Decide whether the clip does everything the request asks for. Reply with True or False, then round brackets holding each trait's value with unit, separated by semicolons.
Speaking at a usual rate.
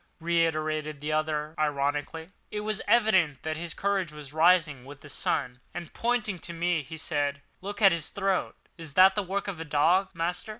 True (185 wpm)